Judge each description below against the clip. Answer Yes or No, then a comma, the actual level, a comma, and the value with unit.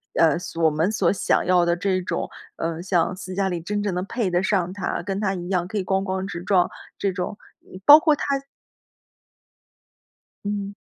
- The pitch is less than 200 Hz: Yes, medium, 185 Hz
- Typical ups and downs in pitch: No, narrow, 2.3 semitones